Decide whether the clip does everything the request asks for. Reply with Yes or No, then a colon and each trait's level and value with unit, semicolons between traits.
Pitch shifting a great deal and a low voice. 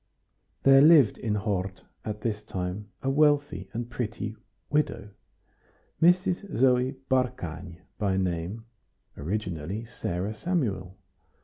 Yes: wide, 6.0 semitones; low, 105 Hz